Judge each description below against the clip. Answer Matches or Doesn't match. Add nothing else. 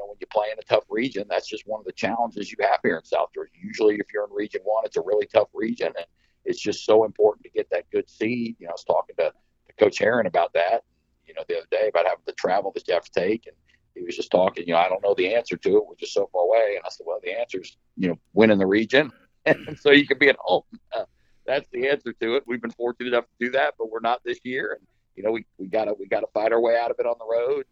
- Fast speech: Matches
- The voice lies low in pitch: Doesn't match